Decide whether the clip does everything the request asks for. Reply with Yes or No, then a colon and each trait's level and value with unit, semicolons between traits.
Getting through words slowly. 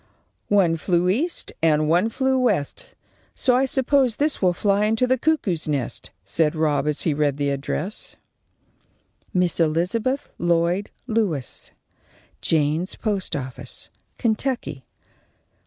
Yes: slow, 125 wpm